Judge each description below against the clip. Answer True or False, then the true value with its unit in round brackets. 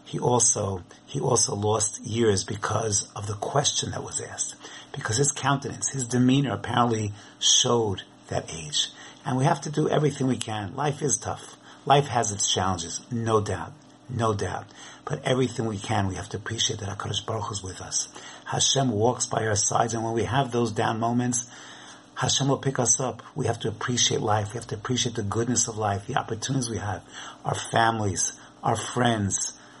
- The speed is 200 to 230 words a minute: False (185 wpm)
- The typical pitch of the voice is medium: False (115 Hz)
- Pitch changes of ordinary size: True (3.2 semitones)